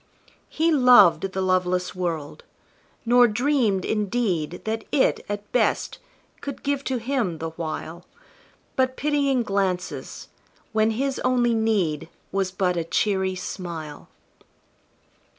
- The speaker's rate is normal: No, slow, 115 wpm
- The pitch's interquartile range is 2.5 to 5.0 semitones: No, wide, 5.6 semitones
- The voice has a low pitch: No, high, 205 Hz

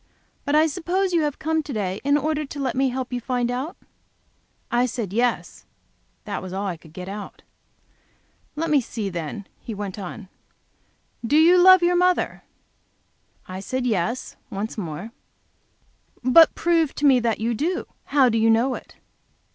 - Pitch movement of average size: No, wide, 6.5 semitones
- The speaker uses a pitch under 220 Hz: No, very high, 250 Hz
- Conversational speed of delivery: Yes, average, 180 wpm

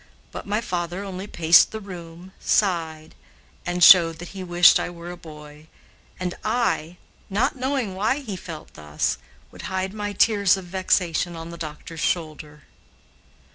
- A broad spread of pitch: No, average, 3.1 semitones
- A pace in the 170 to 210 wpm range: No, average, 155 wpm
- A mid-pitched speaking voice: Yes, medium, 175 Hz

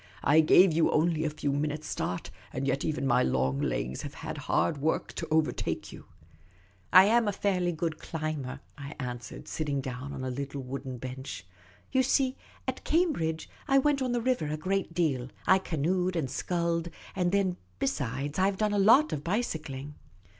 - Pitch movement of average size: No, wide, 5.7 semitones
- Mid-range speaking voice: Yes, medium, 155 Hz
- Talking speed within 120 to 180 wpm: No, average, 200 wpm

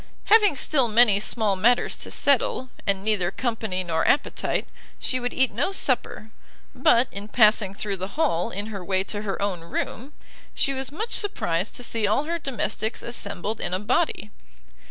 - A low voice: No, high, 220 Hz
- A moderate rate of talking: Yes, average, 175 wpm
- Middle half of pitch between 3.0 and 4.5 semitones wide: No, average, 4.9 semitones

